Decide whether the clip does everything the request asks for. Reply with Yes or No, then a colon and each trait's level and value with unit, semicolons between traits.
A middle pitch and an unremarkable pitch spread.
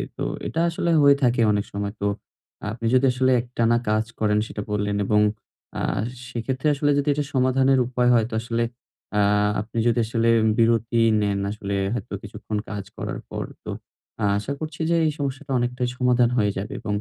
No: low, 120 Hz; average, 3.5 semitones